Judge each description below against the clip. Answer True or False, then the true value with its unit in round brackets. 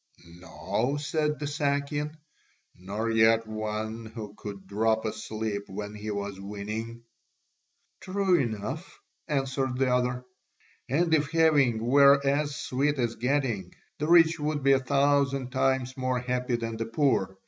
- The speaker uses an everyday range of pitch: True (4.7 semitones)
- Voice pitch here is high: False (125 Hz)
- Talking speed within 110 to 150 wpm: True (135 wpm)